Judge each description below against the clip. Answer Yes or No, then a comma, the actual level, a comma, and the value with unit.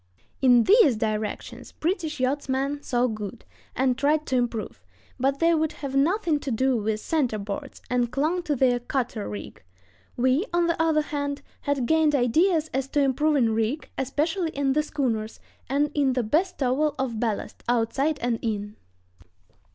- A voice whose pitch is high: Yes, very high, 270 Hz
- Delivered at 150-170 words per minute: Yes, average, 160 wpm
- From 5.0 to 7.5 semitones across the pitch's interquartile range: No, average, 4.0 semitones